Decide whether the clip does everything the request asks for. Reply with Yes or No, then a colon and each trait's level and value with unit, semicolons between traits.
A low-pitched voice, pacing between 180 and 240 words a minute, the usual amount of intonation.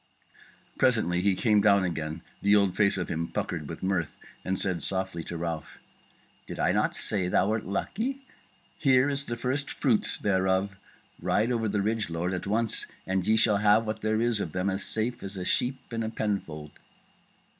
Yes: low, 100 Hz; average, 190 wpm; average, 3.5 semitones